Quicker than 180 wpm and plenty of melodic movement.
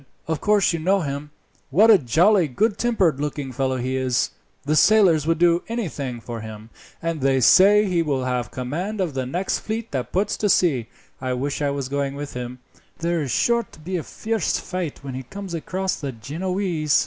Yes: average, 200 wpm; wide, 6.2 semitones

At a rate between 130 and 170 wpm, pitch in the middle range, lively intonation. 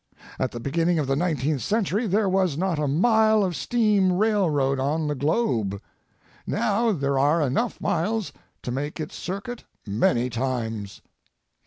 Yes: average, 150 wpm; medium, 160 Hz; wide, 7.0 semitones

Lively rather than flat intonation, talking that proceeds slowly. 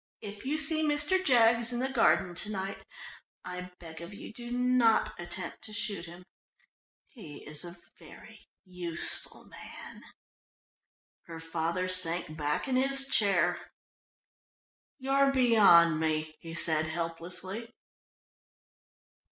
Yes: wide, 6.5 semitones; slow, 120 wpm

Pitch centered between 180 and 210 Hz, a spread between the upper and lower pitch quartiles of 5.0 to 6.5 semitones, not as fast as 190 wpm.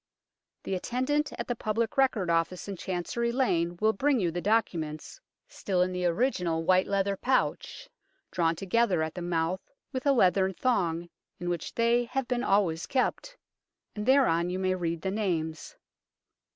Yes: high, 190 Hz; wide, 5.5 semitones; average, 165 wpm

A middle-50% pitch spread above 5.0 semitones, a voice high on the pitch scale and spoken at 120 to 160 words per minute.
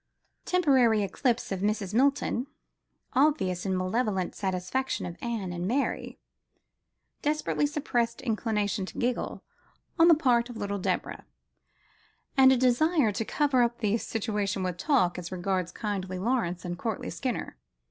Yes: wide, 5.5 semitones; high, 225 Hz; slow, 135 wpm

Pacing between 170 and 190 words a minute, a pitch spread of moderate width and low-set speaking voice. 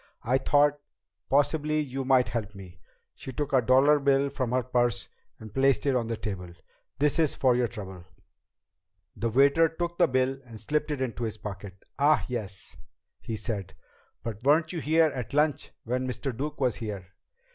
Yes: average, 180 wpm; average, 4.4 semitones; low, 130 Hz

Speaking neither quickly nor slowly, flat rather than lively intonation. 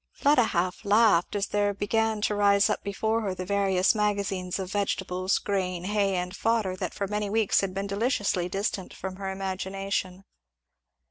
Yes: average, 165 wpm; narrow, 1.8 semitones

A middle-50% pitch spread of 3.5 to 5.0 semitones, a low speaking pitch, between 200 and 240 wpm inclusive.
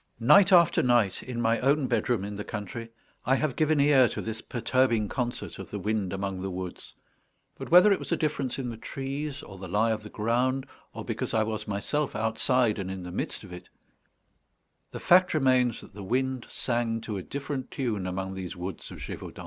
Yes: average, 4.6 semitones; low, 115 Hz; fast, 205 wpm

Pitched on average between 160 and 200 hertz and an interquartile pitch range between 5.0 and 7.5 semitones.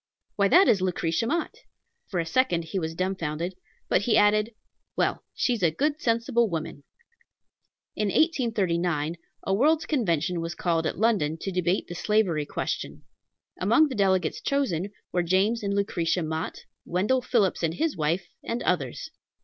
Yes: high, 190 Hz; wide, 5.4 semitones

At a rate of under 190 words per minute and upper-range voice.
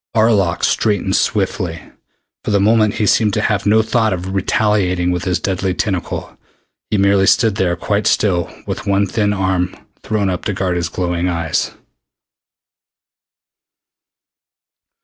No: average, 140 wpm; very low, 95 Hz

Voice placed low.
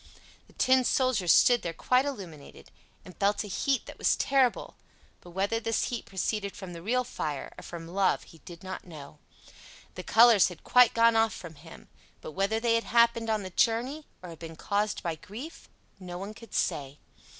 No: high, 205 Hz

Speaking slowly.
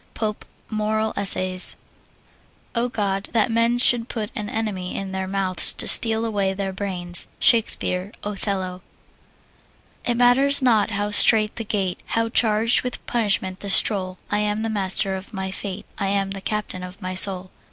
No: average, 165 wpm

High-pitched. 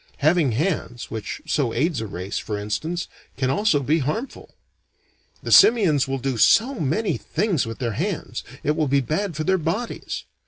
No: medium, 150 Hz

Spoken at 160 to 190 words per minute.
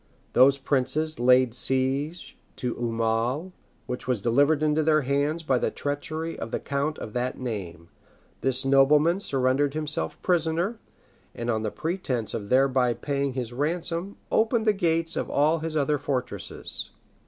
No: average, 145 wpm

